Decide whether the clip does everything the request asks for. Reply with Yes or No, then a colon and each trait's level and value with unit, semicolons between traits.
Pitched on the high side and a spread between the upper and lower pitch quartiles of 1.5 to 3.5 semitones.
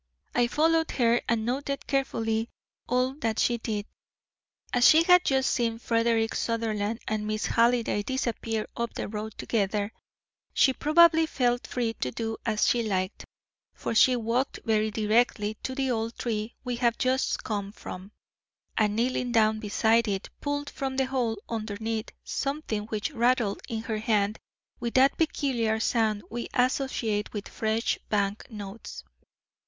Yes: high, 230 Hz; average, 2.8 semitones